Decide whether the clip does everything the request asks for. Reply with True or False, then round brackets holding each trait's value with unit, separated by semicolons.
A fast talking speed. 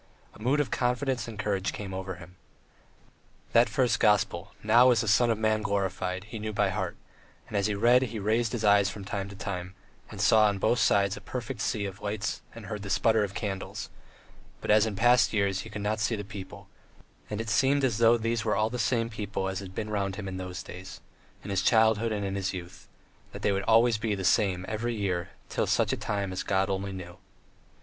True (225 wpm)